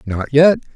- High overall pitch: No, low, 135 Hz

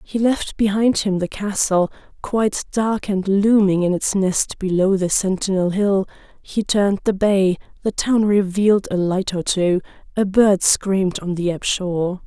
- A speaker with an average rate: Yes, average, 170 wpm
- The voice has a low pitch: No, high, 195 Hz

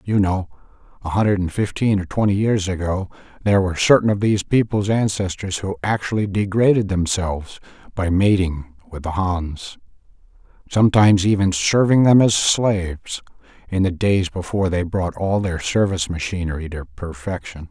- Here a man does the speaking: Yes, male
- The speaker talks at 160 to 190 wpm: No, average, 150 wpm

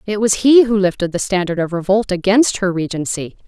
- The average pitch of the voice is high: Yes, high, 195 Hz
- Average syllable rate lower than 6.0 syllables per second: Yes, 5.5 syllables/s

